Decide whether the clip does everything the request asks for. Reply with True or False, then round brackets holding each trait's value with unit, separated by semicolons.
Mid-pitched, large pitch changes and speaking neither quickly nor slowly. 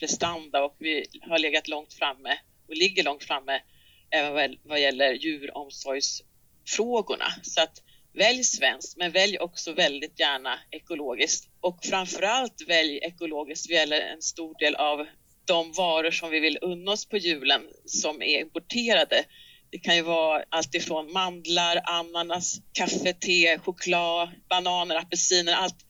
False (170 Hz; 2.6 semitones; 140 wpm)